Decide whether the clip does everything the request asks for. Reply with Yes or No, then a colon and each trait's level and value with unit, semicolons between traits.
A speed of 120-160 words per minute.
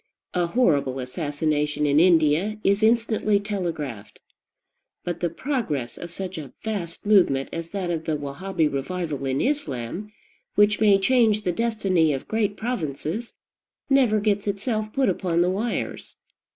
Yes: average, 140 wpm